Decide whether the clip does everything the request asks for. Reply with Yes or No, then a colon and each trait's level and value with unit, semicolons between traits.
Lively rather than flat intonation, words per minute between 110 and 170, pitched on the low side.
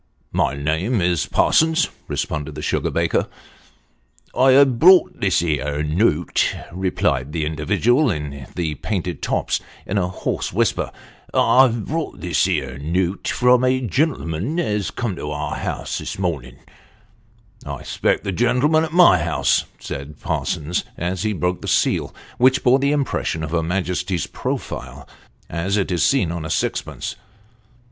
Yes: wide, 8.0 semitones; average, 155 wpm; very low, 90 Hz